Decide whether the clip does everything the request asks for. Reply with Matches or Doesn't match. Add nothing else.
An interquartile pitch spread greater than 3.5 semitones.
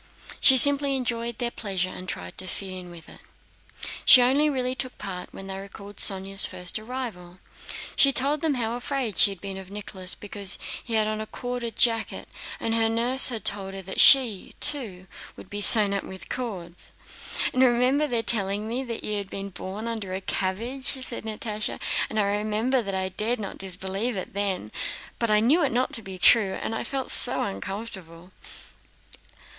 Matches